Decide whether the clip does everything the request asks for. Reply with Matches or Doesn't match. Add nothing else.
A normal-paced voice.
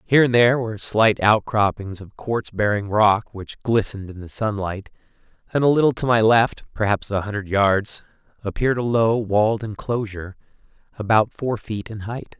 Matches